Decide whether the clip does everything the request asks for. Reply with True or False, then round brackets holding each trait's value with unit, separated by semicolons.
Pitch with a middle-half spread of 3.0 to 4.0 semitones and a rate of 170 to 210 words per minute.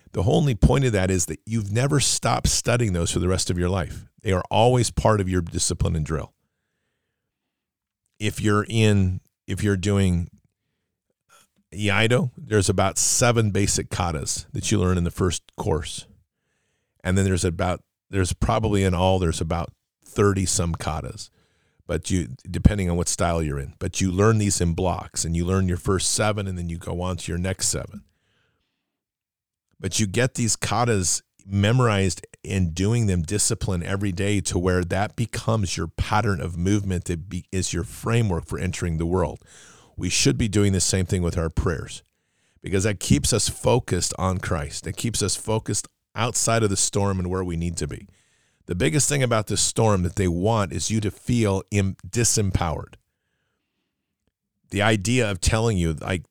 True (3.4 semitones; 180 wpm)